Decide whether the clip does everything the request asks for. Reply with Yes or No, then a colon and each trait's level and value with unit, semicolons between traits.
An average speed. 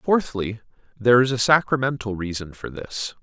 Yes: average, 150 wpm